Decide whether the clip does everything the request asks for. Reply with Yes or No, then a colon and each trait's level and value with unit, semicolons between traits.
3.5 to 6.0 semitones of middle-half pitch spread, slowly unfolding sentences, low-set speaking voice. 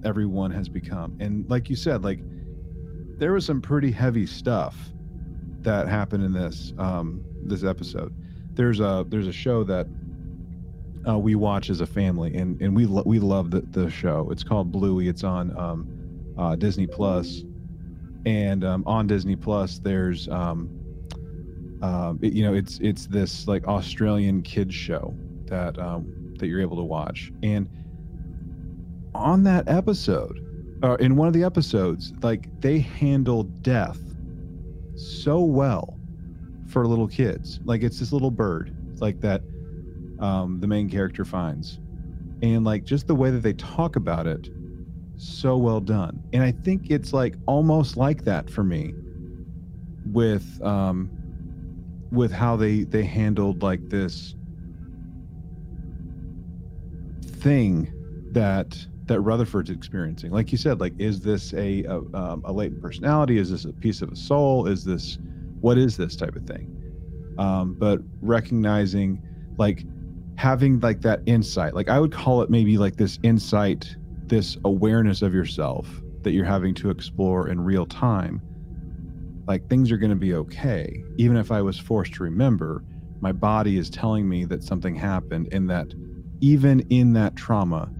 No: average, 4.4 semitones; average, 155 wpm; very low, 95 Hz